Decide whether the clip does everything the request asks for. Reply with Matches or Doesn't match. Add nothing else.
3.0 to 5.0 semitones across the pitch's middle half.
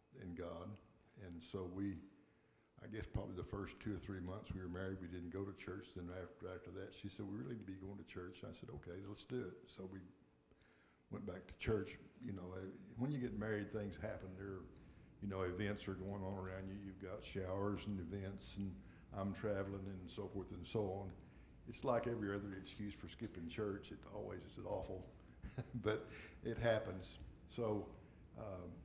Doesn't match